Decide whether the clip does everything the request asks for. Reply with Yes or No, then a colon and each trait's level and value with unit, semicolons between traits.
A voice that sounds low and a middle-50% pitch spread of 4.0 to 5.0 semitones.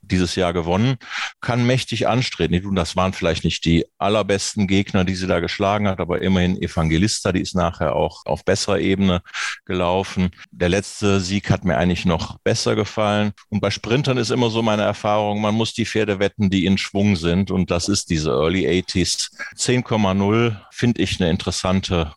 No: low, 100 Hz; average, 2.8 semitones